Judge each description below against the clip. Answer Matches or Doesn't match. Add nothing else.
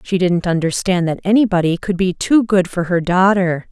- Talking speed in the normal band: Matches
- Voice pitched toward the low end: Doesn't match